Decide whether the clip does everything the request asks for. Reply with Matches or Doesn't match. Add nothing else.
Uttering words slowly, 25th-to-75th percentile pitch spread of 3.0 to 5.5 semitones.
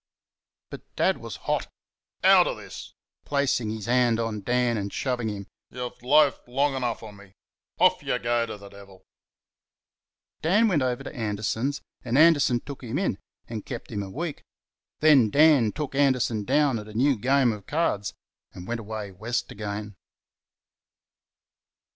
Doesn't match